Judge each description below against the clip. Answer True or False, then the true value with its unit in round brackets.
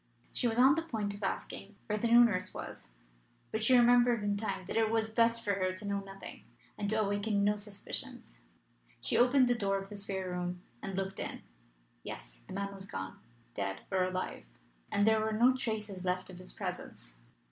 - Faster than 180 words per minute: True (200 wpm)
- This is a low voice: False (205 Hz)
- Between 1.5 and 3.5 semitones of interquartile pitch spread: True (2.8 semitones)